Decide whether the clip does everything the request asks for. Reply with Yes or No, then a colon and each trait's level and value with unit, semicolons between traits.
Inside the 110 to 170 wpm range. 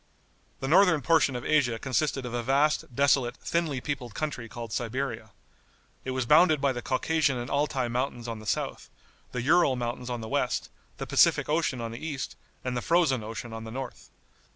No: average, 190 wpm